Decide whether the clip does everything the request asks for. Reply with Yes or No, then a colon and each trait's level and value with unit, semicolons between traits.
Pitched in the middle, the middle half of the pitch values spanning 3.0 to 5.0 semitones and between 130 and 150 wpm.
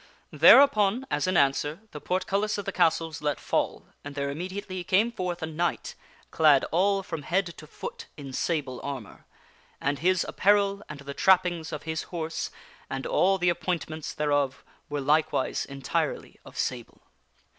No: medium, 160 Hz; average, 4.4 semitones; average, 165 wpm